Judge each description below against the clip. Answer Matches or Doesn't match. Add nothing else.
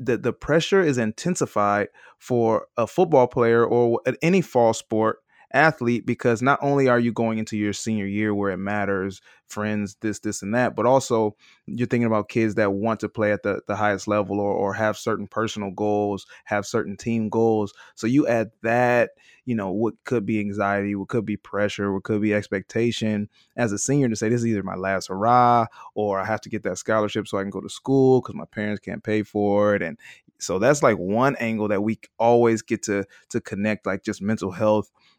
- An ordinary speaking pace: Doesn't match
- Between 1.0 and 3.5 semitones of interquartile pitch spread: Matches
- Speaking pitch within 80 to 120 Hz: Matches